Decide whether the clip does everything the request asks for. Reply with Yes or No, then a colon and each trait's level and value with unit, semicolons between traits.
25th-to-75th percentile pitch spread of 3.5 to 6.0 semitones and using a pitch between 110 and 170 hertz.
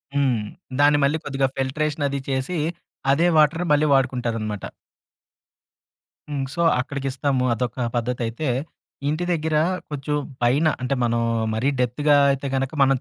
No: average, 2.7 semitones; low, 135 Hz